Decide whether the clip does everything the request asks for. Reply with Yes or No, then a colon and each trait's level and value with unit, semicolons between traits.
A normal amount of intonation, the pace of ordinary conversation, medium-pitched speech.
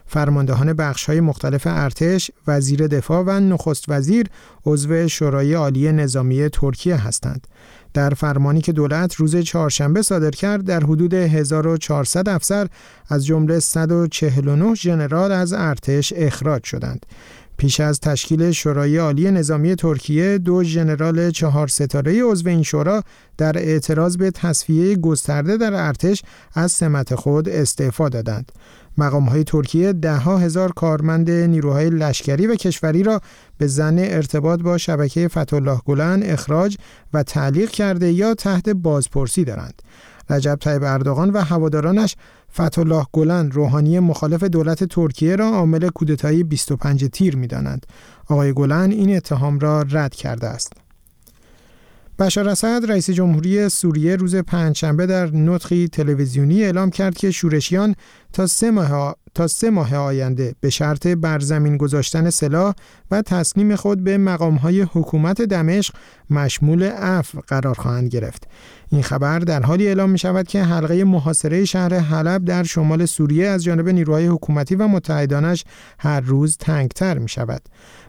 Yes: average, 3.7 semitones; average, 135 wpm; medium, 160 Hz